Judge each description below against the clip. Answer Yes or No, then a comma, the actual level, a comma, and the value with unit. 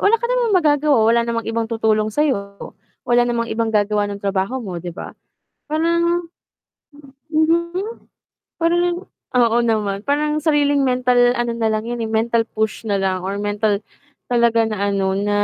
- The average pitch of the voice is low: No, high, 235 Hz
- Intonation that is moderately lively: No, wide, 6.0 semitones